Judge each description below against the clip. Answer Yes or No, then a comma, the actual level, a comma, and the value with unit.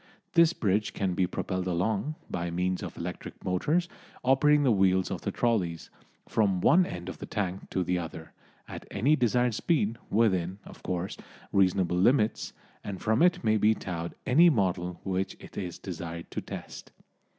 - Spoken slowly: No, average, 170 wpm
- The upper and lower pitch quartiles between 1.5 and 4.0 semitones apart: No, average, 4.7 semitones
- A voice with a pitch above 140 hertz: No, very low, 95 Hz